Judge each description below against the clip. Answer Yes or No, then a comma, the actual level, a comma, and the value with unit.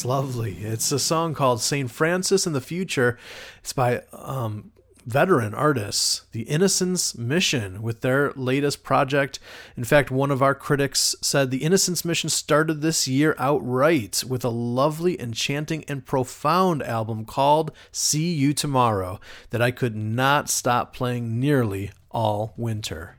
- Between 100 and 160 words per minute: Yes, average, 145 wpm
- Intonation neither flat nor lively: Yes, average, 4.3 semitones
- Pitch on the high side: No, low, 135 Hz